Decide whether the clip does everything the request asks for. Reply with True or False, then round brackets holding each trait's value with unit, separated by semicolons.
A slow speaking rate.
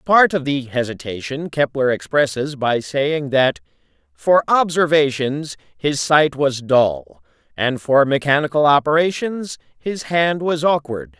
True (125 wpm)